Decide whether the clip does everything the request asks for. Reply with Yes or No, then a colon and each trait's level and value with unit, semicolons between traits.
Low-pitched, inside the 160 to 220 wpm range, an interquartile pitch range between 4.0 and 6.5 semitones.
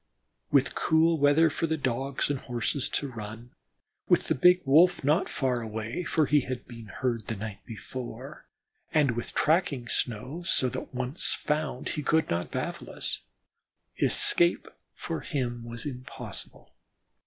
No: low, 130 Hz; average, 150 wpm; average, 4.5 semitones